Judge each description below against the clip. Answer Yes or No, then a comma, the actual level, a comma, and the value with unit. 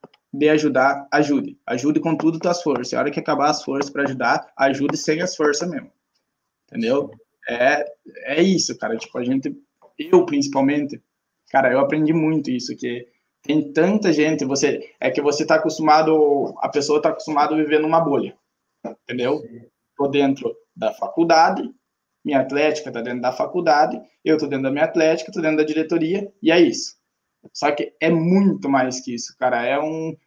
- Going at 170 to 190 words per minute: Yes, average, 175 wpm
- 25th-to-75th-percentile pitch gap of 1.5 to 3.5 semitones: Yes, average, 3.2 semitones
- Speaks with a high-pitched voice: No, medium, 155 Hz